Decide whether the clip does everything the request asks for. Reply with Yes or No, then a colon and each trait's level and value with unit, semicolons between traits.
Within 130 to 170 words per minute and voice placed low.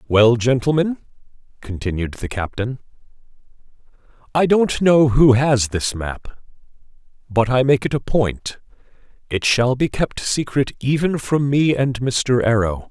Yes: slow, 135 wpm; low, 125 Hz